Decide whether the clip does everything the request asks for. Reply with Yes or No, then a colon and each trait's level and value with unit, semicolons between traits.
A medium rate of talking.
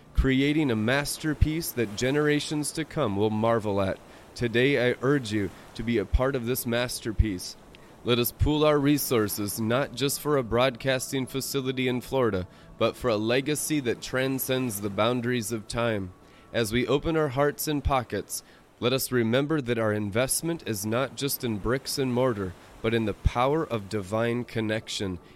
Yes: average, 170 wpm